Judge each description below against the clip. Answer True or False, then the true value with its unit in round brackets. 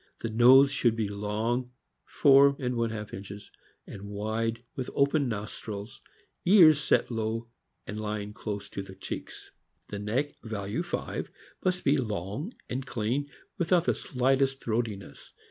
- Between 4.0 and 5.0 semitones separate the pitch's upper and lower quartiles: True (4.4 semitones)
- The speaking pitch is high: False (115 Hz)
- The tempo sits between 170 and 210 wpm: False (145 wpm)